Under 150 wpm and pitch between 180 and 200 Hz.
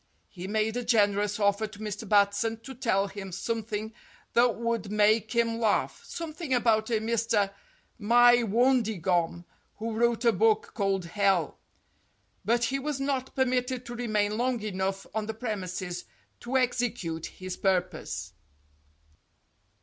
No: slow, 135 wpm; high, 220 Hz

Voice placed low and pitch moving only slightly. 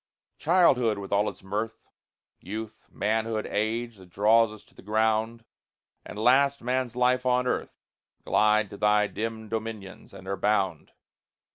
Yes: low, 110 Hz; narrow, 2.0 semitones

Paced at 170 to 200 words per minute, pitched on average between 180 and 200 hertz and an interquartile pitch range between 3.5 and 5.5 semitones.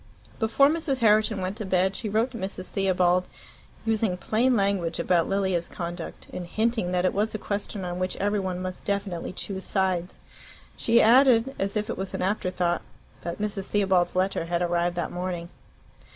No: average, 180 wpm; high, 190 Hz; average, 3.0 semitones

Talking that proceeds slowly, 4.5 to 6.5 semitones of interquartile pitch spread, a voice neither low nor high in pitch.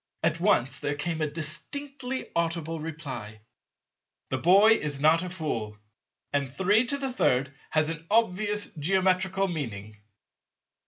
Yes: slow, 115 wpm; average, 5.1 semitones; medium, 165 Hz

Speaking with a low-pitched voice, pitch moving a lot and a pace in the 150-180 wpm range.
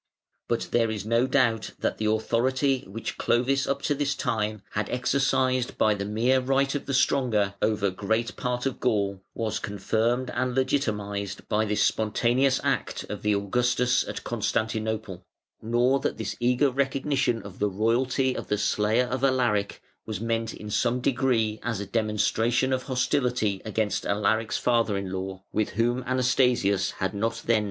No: low, 115 Hz; average, 3.4 semitones; average, 165 wpm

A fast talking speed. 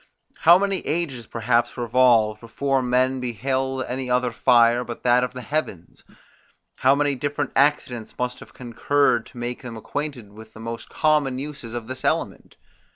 No: average, 160 wpm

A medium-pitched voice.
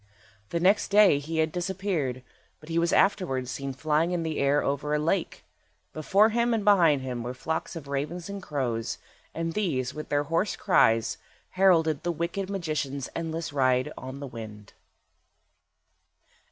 Yes: medium, 155 Hz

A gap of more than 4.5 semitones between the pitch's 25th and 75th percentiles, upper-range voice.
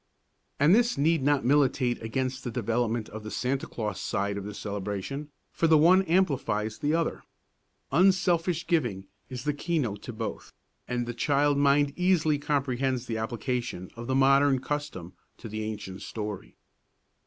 No: average, 5.0 semitones; low, 130 Hz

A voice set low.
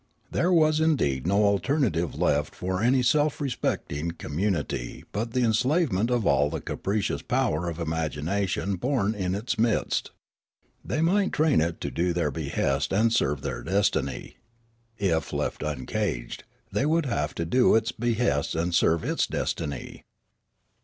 Yes: low, 100 Hz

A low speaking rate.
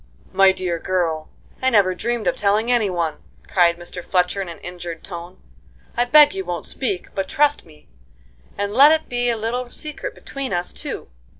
No: average, 185 wpm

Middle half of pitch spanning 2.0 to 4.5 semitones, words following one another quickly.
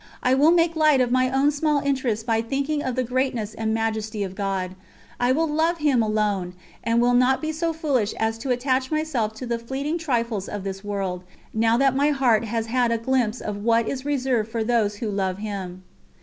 Yes: average, 4.0 semitones; fast, 210 wpm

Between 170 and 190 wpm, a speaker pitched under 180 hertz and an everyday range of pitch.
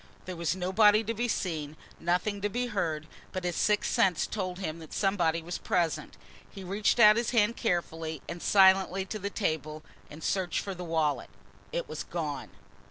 No: average, 180 wpm; medium, 185 Hz; average, 4.0 semitones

